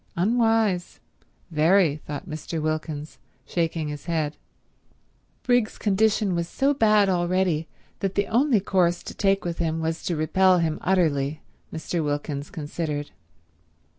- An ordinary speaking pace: No, slow, 130 wpm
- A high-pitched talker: No, medium, 170 Hz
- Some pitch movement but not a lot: Yes, average, 3.9 semitones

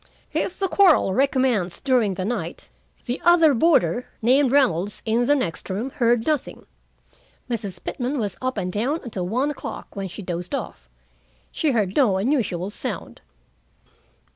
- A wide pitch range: Yes, wide, 6.2 semitones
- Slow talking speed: No, average, 150 wpm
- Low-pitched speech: No, high, 235 Hz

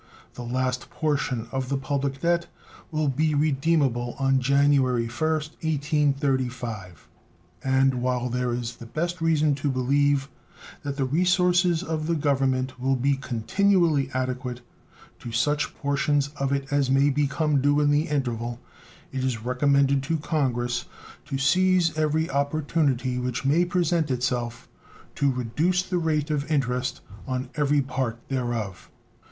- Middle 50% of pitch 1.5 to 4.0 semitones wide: Yes, average, 3.1 semitones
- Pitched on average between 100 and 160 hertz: Yes, medium, 140 Hz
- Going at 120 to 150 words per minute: Yes, average, 140 wpm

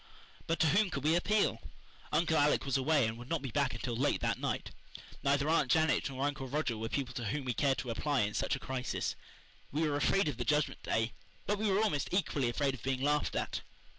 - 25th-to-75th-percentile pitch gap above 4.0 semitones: No, average, 3.5 semitones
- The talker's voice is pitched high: No, medium, 140 Hz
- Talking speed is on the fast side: Yes, fast, 230 wpm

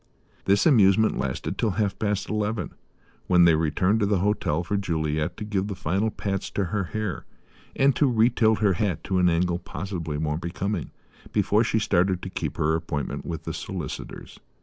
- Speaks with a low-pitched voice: Yes, very low, 95 Hz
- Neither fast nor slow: Yes, average, 180 wpm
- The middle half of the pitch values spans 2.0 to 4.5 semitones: Yes, average, 3.7 semitones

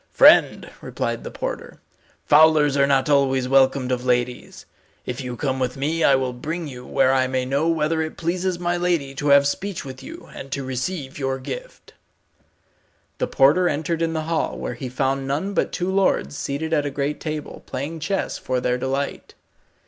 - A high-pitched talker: No, medium, 140 Hz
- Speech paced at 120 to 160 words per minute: No, average, 185 wpm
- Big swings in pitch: No, average, 3.5 semitones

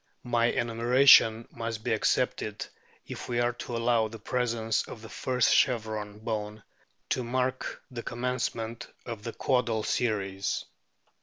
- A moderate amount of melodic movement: No, narrow, 1.8 semitones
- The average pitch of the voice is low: Yes, low, 115 Hz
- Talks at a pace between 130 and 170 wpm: Yes, average, 140 wpm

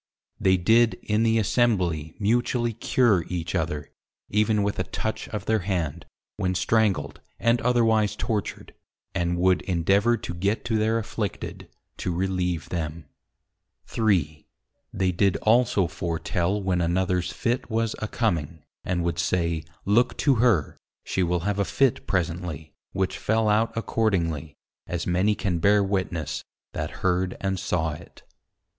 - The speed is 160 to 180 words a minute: No, average, 145 wpm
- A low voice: Yes, very low, 95 Hz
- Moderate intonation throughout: Yes, average, 4.2 semitones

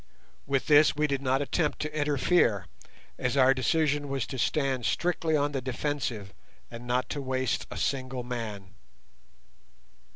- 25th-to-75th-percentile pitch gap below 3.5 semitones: Yes, average, 2.7 semitones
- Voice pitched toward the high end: No, low, 135 Hz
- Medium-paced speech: Yes, average, 150 wpm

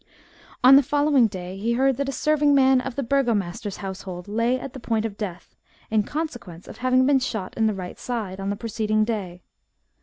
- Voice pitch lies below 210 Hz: No, high, 230 Hz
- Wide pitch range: No, average, 5.0 semitones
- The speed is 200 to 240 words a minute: Yes, fast, 205 wpm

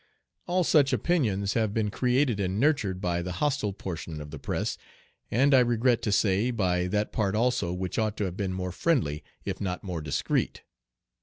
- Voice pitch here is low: Yes, low, 105 Hz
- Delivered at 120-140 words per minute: No, average, 185 wpm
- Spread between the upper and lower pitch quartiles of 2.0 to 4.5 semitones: No, average, 5.1 semitones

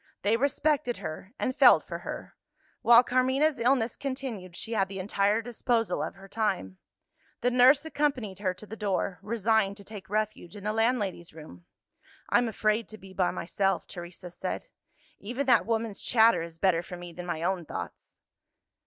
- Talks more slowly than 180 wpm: Yes, average, 170 wpm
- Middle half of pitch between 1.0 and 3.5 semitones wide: No, average, 4.4 semitones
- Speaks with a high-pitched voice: Yes, high, 215 Hz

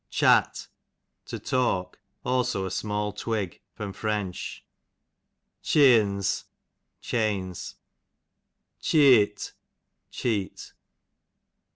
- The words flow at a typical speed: No, slow, 60 wpm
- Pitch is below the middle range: Yes, low, 105 Hz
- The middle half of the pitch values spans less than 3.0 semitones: No, average, 3.5 semitones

